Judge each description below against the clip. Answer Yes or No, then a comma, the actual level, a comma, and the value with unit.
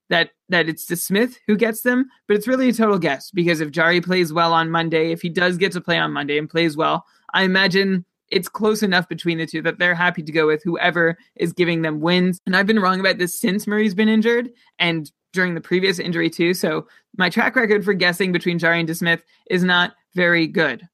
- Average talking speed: No, fast, 235 wpm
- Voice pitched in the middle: Yes, medium, 180 Hz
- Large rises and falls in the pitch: No, average, 2.8 semitones